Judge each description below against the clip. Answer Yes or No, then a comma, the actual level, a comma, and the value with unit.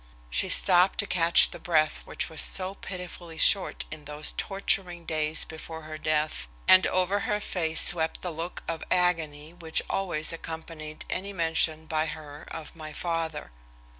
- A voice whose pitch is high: No, medium, 165 Hz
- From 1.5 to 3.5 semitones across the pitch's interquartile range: Yes, narrow, 2.4 semitones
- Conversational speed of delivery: Yes, average, 160 wpm